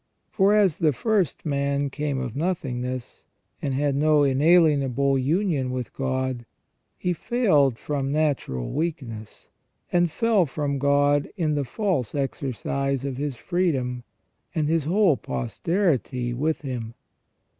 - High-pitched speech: No, medium, 140 Hz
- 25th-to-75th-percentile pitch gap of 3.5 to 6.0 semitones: Yes, average, 3.8 semitones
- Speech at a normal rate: No, slow, 125 wpm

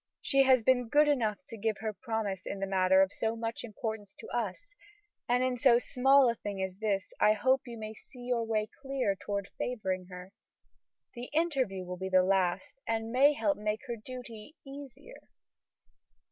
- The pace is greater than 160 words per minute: Yes, average, 190 wpm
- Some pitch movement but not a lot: Yes, average, 4.5 semitones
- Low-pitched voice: No, high, 225 Hz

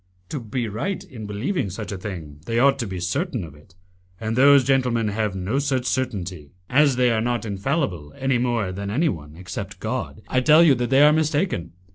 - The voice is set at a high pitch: No, low, 120 Hz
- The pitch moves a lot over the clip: Yes, wide, 5.8 semitones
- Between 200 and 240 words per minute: Yes, fast, 205 wpm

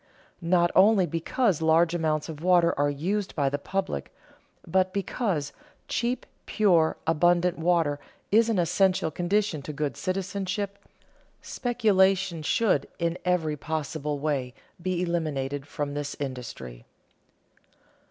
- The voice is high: No, medium, 170 Hz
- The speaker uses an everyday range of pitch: Yes, average, 4.3 semitones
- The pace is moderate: No, slow, 120 wpm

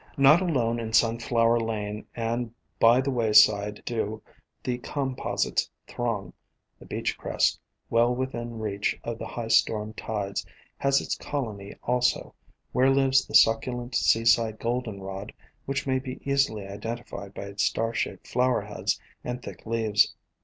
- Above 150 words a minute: No, average, 145 wpm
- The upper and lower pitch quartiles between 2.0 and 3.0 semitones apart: Yes, narrow, 2.6 semitones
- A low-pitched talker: Yes, low, 115 Hz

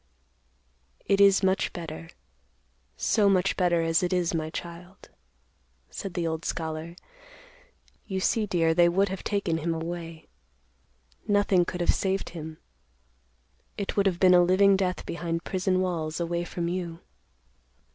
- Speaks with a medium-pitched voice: Yes, medium, 175 Hz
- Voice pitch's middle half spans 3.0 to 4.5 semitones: No, narrow, 2.4 semitones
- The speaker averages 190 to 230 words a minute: No, average, 145 wpm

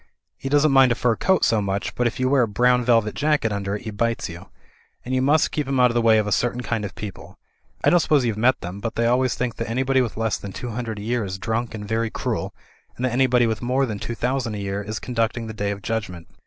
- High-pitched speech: No, low, 115 Hz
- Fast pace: Yes, fast, 275 wpm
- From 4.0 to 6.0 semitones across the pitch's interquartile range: No, average, 2.9 semitones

